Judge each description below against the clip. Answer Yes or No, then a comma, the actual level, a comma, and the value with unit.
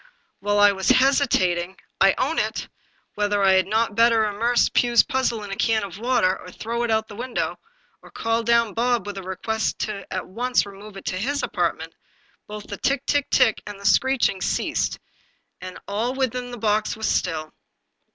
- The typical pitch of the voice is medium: No, high, 220 Hz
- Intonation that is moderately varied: Yes, average, 3.4 semitones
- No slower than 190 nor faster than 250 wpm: Yes, average, 200 wpm